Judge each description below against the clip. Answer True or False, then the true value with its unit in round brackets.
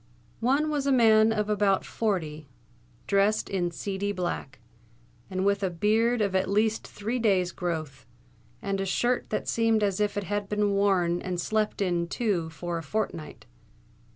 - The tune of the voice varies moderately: True (3.3 semitones)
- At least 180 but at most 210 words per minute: False (165 wpm)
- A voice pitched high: True (200 Hz)